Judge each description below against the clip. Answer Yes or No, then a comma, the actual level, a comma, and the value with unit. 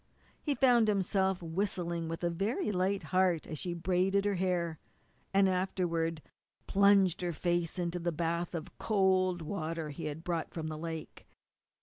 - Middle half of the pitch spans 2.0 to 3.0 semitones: Yes, narrow, 2.5 semitones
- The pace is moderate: Yes, average, 155 wpm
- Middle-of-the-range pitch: Yes, medium, 175 Hz